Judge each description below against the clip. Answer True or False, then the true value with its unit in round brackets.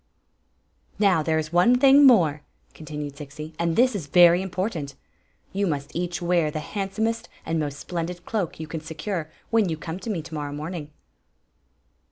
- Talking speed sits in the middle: True (175 wpm)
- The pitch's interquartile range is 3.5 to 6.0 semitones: True (4.0 semitones)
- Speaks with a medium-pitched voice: True (170 Hz)